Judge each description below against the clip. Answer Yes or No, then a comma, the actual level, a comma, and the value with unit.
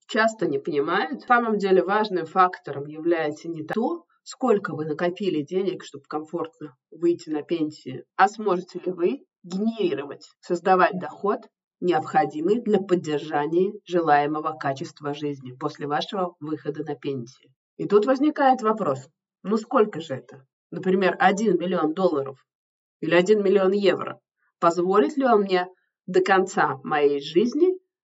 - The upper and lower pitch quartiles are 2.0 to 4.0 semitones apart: No, average, 5.3 semitones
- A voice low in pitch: No, medium, 180 Hz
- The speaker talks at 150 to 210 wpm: No, average, 135 wpm